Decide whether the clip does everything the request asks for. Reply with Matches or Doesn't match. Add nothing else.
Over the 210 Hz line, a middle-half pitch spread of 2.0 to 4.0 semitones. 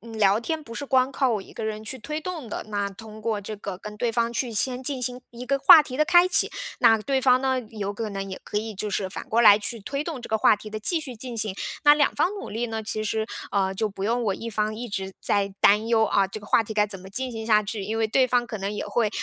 Matches